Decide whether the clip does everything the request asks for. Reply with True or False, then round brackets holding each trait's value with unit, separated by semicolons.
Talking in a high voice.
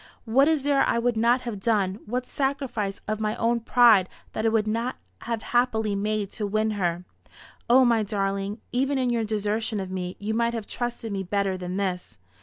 True (220 Hz)